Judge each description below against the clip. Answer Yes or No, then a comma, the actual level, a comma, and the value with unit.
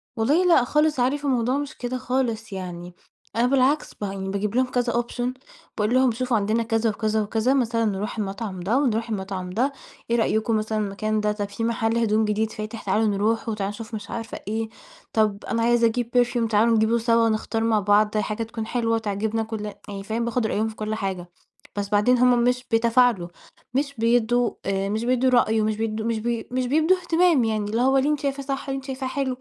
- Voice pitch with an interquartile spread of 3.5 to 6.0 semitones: No, average, 2.7 semitones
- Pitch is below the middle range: No, high, 225 Hz